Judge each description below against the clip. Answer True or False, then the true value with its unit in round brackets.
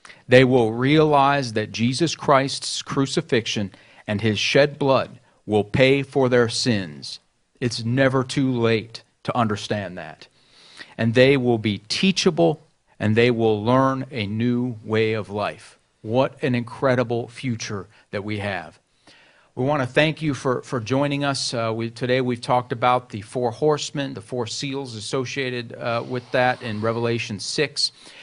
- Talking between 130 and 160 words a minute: True (155 wpm)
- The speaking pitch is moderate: False (125 Hz)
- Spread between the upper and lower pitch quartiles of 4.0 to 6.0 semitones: False (3.3 semitones)